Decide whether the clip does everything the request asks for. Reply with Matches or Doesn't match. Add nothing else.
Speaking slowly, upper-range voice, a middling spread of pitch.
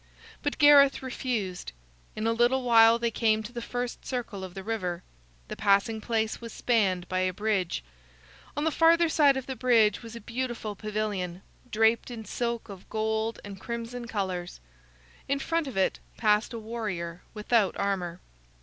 Doesn't match